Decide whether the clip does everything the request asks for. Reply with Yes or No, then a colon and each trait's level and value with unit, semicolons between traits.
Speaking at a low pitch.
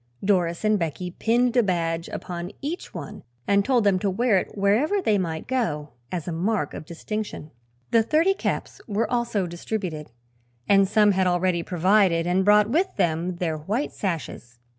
No: high, 195 Hz